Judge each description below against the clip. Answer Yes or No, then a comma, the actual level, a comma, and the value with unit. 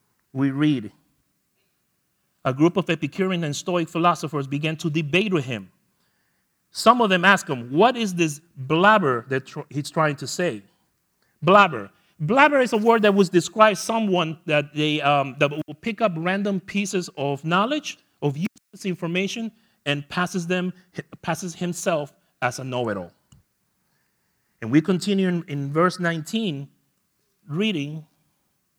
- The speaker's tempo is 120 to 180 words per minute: Yes, average, 140 wpm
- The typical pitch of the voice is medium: Yes, medium, 170 Hz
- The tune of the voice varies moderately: Yes, average, 5.0 semitones